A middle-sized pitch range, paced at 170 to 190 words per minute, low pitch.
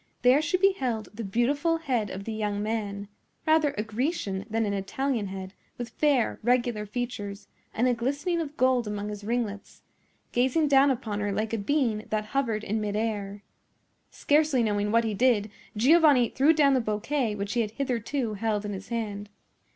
No: average, 4.3 semitones; average, 175 wpm; high, 225 Hz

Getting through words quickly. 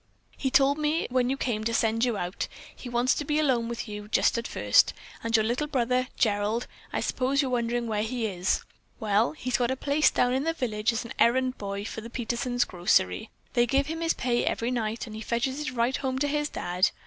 Yes: fast, 220 wpm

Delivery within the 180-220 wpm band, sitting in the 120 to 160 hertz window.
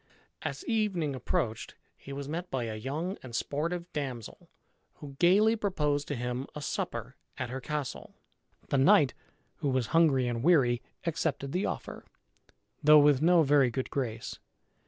No: average, 155 wpm; medium, 140 Hz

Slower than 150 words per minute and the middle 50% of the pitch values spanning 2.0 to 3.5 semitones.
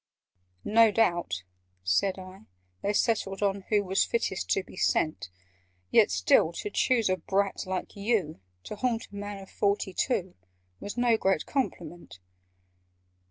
Yes: average, 140 wpm; average, 3.1 semitones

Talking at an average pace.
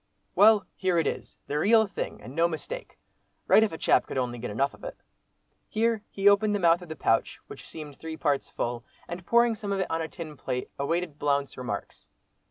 No: fast, 210 wpm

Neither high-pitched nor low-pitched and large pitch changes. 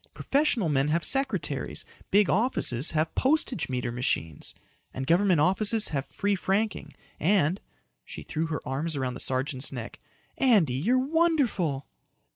Yes: medium, 165 Hz; wide, 8.3 semitones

